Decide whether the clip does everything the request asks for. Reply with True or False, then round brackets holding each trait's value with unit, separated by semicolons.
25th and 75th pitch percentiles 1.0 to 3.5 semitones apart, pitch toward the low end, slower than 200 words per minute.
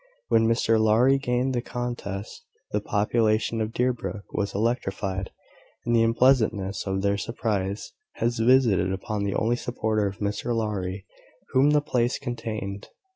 True (3.1 semitones; 110 Hz; 140 wpm)